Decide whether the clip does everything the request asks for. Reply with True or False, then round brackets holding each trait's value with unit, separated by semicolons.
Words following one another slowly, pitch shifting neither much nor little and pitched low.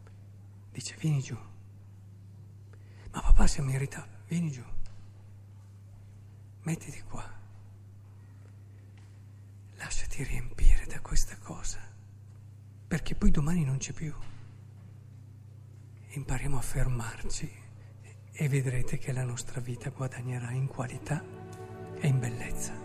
True (95 wpm; 4.3 semitones; 105 Hz)